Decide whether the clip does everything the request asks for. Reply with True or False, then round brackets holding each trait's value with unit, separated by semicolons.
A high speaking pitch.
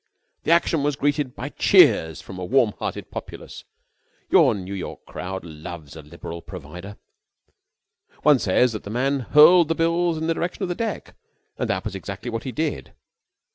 False (120 Hz)